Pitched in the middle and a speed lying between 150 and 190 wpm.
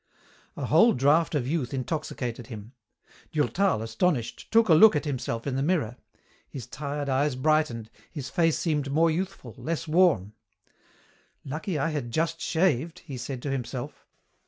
Yes: medium, 145 Hz; average, 155 wpm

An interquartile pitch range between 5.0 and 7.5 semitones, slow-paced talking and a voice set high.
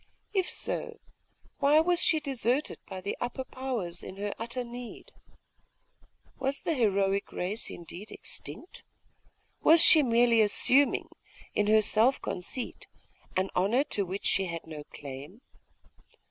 Yes: wide, 5.5 semitones; slow, 130 wpm; high, 225 Hz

